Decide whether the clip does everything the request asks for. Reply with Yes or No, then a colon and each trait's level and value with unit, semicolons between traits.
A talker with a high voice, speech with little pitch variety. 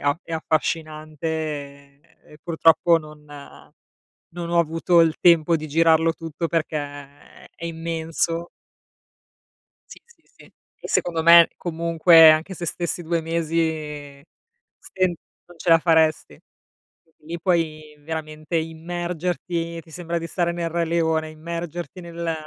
No: medium, 165 Hz; narrow, 1.4 semitones